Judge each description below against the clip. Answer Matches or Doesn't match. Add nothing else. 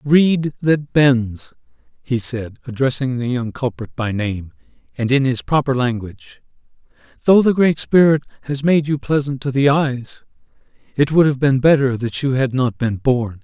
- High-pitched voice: Doesn't match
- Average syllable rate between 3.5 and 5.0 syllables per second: Matches